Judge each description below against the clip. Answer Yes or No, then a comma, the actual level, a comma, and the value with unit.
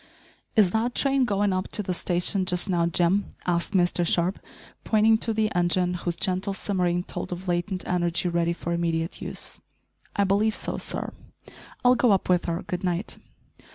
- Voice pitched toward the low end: No, medium, 180 Hz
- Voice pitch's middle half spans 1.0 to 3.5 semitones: Yes, average, 2.7 semitones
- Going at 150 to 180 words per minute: Yes, average, 175 wpm